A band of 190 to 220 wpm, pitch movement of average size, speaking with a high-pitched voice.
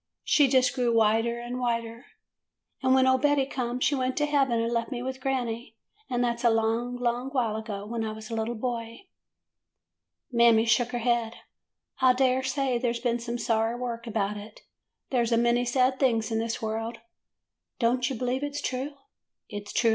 No: average, 195 wpm; narrow, 2.1 semitones; high, 240 Hz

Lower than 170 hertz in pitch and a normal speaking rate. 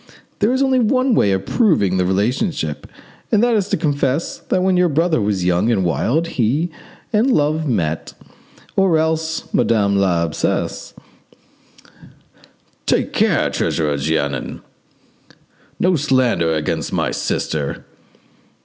No: low, 135 Hz; slow, 125 wpm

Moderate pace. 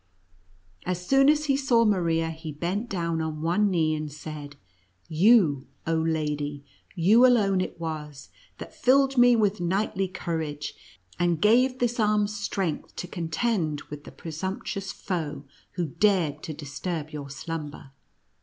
Yes: average, 150 wpm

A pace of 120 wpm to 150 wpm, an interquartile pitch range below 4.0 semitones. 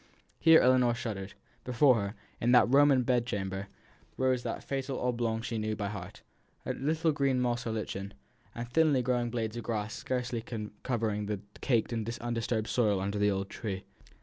No: average, 175 wpm; average, 3.1 semitones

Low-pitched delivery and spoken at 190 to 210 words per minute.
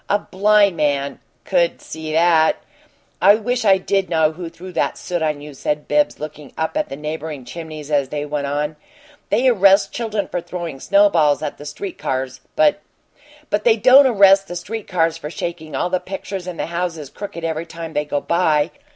No: medium, 170 Hz; average, 195 wpm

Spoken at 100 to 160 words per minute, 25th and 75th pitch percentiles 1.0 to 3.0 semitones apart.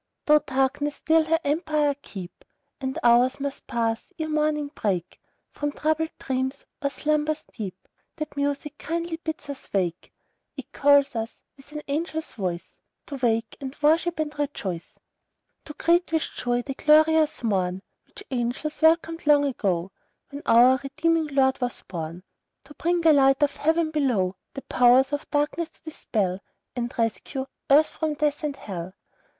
No: average, 155 wpm; average, 4.2 semitones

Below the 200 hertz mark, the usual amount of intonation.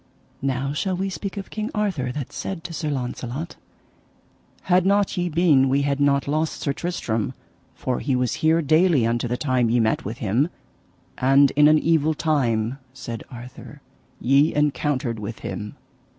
Yes: medium, 140 Hz; average, 4.7 semitones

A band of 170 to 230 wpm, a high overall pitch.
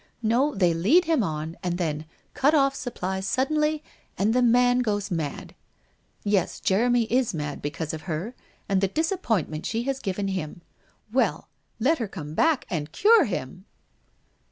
No: average, 155 wpm; high, 205 Hz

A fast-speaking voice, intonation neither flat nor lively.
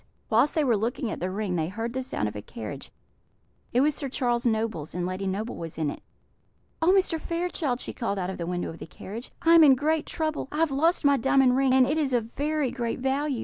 No: fast, 245 wpm; wide, 6.7 semitones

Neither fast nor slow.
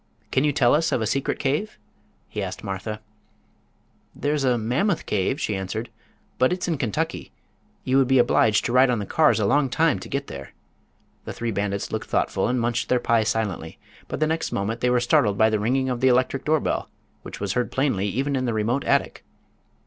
No: fast, 210 wpm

